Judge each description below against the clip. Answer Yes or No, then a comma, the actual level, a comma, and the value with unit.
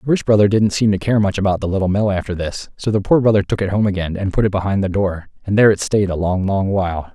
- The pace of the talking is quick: Yes, fast, 300 wpm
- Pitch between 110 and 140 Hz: No, low, 100 Hz